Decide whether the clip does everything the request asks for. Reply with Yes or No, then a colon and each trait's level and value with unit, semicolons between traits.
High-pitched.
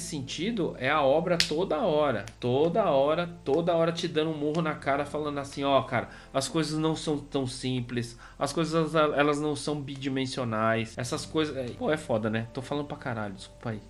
No: medium, 140 Hz